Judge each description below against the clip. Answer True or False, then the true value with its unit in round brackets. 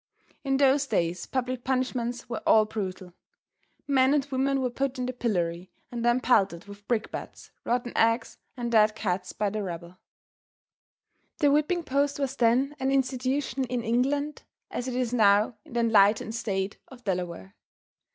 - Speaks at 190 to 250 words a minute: False (160 wpm)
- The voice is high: True (240 Hz)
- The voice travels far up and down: False (4.4 semitones)